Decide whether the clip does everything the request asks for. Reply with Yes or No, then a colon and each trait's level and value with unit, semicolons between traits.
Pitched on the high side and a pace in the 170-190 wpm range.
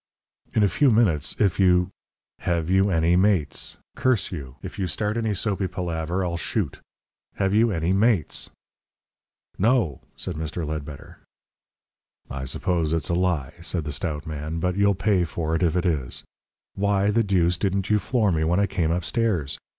No: very low, 90 Hz; average, 175 wpm